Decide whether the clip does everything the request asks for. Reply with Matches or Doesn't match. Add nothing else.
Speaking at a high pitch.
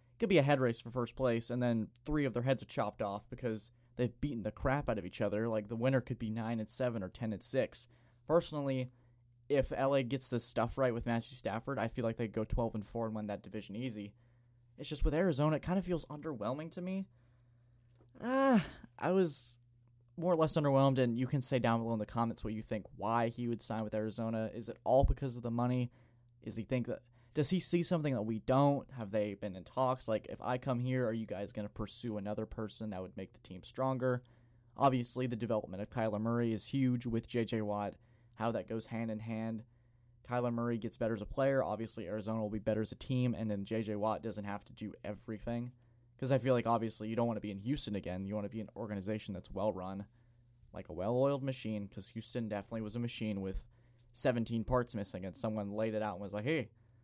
Doesn't match